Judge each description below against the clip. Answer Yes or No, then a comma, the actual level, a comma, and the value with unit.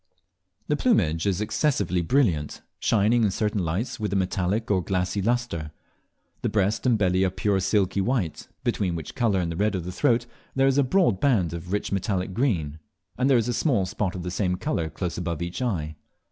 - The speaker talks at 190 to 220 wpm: Yes, average, 200 wpm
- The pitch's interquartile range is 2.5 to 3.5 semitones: No, average, 4.6 semitones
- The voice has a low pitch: Yes, very low, 95 Hz